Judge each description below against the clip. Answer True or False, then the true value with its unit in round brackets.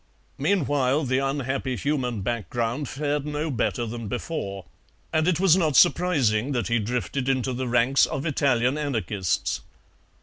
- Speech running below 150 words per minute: True (140 wpm)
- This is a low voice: True (130 Hz)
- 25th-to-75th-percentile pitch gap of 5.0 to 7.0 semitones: False (3.8 semitones)